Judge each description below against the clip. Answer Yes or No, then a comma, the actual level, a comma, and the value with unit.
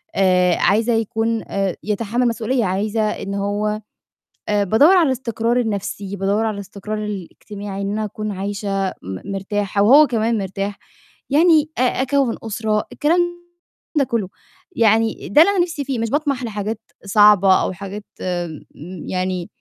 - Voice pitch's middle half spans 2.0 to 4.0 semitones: Yes, average, 2.8 semitones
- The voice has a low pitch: No, high, 210 Hz